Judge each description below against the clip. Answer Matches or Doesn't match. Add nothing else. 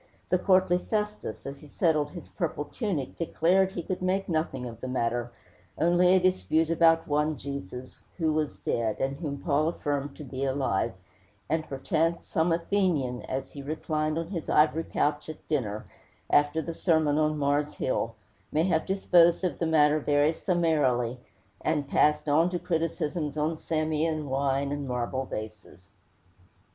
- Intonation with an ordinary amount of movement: Matches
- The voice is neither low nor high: Matches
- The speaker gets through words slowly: Doesn't match